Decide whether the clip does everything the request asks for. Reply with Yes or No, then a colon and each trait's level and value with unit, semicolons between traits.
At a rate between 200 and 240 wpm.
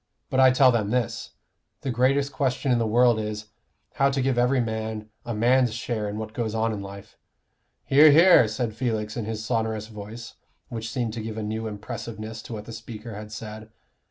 Yes: fast, 205 wpm